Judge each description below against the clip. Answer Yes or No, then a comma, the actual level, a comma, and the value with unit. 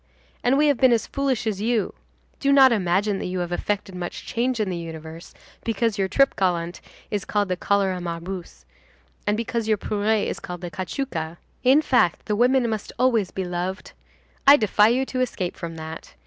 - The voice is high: Yes, high, 205 Hz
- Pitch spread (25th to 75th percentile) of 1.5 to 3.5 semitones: No, average, 5.0 semitones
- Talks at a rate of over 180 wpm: Yes, average, 190 wpm